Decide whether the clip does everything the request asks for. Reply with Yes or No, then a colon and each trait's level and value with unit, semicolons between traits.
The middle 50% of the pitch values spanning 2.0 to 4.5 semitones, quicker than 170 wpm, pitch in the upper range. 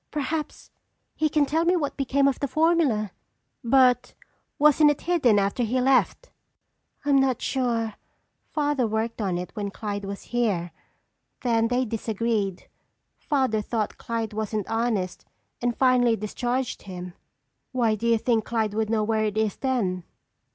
No: average, 3.8 semitones; average, 150 wpm; high, 235 Hz